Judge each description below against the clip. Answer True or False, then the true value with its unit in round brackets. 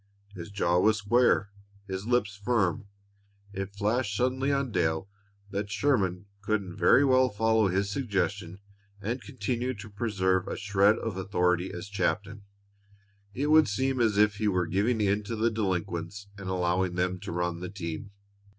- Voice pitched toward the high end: False (100 Hz)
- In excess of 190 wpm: False (160 wpm)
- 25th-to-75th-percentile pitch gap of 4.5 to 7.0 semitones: False (3.3 semitones)